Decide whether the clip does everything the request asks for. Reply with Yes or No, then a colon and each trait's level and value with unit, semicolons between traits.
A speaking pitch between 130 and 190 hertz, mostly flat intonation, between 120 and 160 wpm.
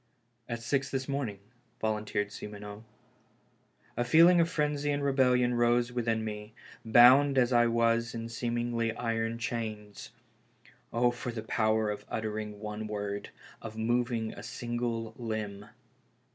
No: low, 115 Hz; narrow, 2.0 semitones; slow, 135 wpm